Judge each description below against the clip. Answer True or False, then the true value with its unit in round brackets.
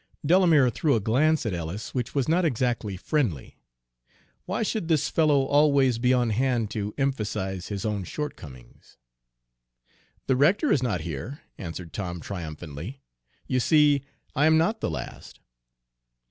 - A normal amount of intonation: False (7.2 semitones)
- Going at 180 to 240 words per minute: False (145 wpm)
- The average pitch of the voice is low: True (125 Hz)